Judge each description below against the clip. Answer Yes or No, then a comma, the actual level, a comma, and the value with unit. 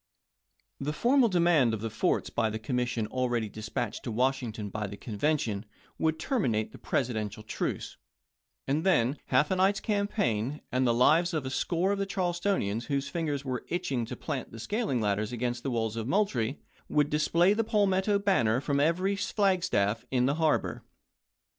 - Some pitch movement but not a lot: No, wide, 7.7 semitones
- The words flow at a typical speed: Yes, average, 170 wpm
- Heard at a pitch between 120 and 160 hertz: Yes, low, 135 Hz